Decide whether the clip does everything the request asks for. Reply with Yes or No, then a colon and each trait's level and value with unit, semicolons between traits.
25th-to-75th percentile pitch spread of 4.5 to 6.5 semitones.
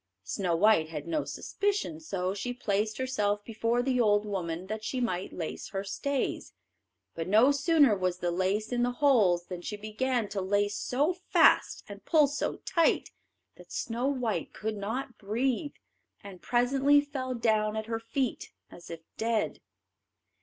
Yes: average, 4.8 semitones